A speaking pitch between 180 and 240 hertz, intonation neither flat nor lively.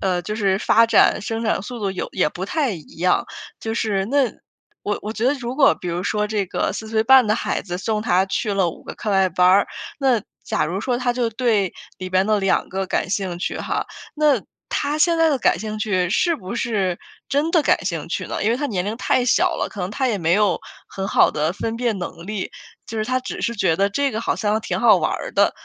Yes: high, 215 Hz; average, 4.2 semitones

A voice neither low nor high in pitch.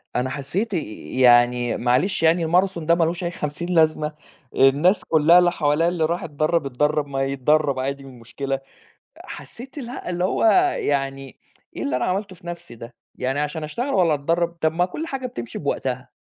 Yes: medium, 155 Hz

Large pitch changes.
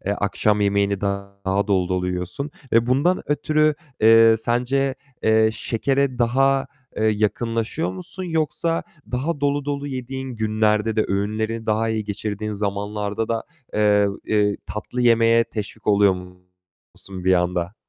No: average, 3.8 semitones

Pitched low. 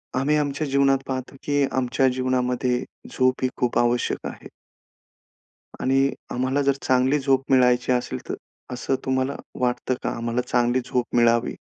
Yes: low, 130 Hz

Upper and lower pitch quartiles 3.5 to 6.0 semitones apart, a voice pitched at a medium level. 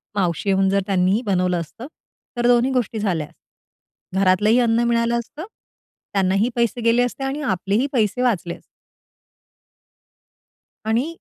No: average, 4.0 semitones; high, 220 Hz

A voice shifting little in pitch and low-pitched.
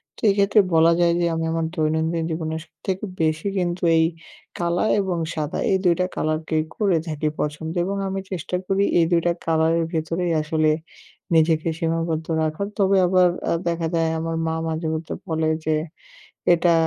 No: narrow, 1.8 semitones; medium, 165 Hz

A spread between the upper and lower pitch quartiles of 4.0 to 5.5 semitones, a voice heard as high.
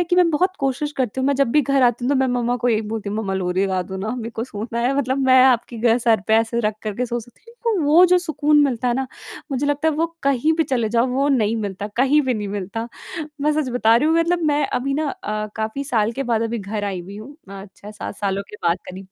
Yes: average, 4.5 semitones; high, 245 Hz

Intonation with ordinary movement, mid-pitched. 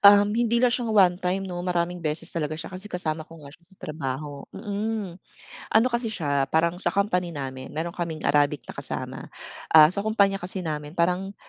Yes: average, 4.4 semitones; medium, 175 Hz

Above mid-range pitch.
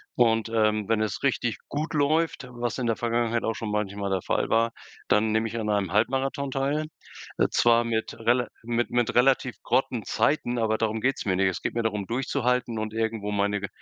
No: low, 115 Hz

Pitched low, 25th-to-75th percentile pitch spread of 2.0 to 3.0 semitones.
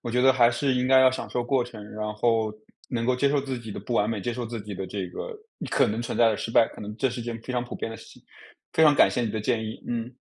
Yes: low, 120 Hz; narrow, 2.5 semitones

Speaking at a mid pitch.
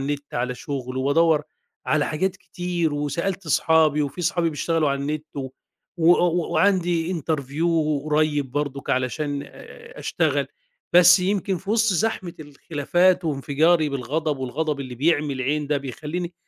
Yes: medium, 155 Hz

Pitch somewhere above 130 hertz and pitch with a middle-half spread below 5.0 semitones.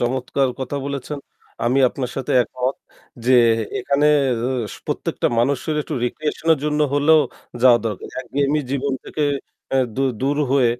Yes: medium, 140 Hz; narrow, 2.4 semitones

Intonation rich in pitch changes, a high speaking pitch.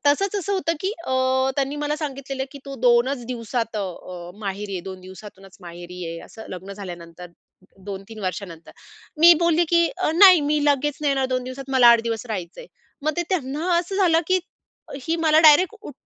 Yes: wide, 8.3 semitones; very high, 260 Hz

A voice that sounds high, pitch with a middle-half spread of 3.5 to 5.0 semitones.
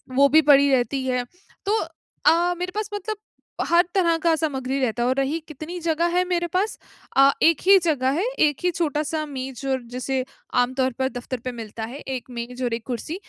Yes: very high, 280 Hz; average, 4.7 semitones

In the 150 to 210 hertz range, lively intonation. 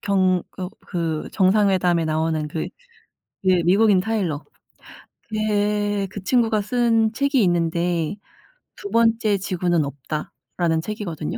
No: high, 190 Hz; average, 4.1 semitones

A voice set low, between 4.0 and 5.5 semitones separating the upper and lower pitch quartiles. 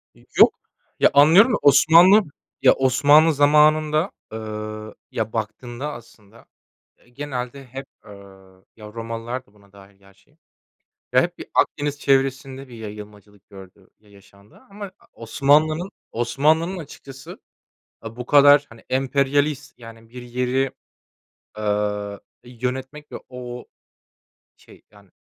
Yes: low, 125 Hz; average, 4.8 semitones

